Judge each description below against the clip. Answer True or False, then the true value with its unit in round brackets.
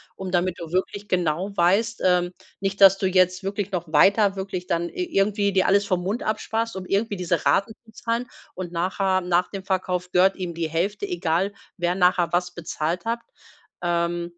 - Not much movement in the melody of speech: True (2.3 semitones)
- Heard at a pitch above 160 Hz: True (185 Hz)